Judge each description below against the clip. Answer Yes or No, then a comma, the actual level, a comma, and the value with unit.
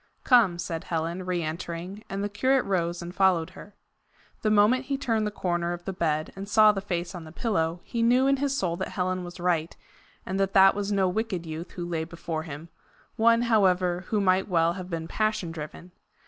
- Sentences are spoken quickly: Yes, fast, 210 wpm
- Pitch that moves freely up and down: No, average, 3.5 semitones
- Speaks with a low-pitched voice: No, medium, 185 Hz